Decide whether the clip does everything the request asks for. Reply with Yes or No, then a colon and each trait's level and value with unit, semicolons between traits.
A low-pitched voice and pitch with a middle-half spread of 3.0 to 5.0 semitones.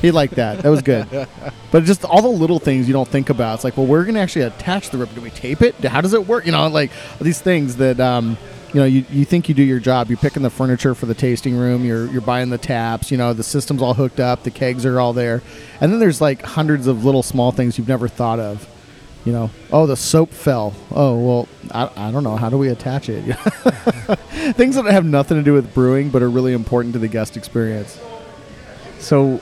Yes: low, 130 Hz; average, 3.5 semitones